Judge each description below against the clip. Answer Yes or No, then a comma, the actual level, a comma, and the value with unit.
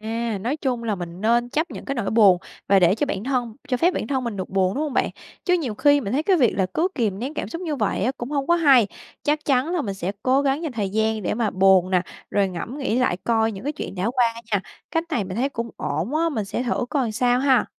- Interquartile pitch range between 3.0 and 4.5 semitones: No, wide, 5.6 semitones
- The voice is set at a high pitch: Yes, high, 235 Hz